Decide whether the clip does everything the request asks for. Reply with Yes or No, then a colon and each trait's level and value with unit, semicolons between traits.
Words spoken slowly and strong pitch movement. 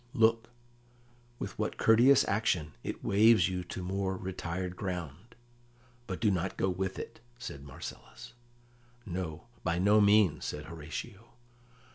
No: slow, 130 wpm; average, 3.8 semitones